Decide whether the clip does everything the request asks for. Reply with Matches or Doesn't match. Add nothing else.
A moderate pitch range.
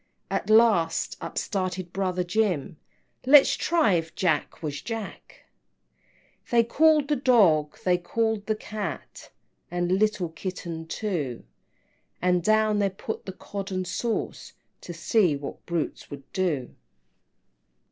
Matches